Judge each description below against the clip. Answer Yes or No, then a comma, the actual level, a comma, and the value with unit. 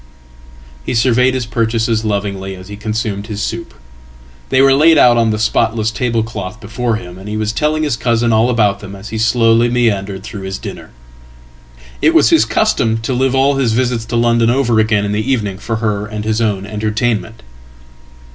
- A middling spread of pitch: No, narrow, 2.2 semitones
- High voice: No, low, 110 Hz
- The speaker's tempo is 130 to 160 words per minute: No, average, 175 wpm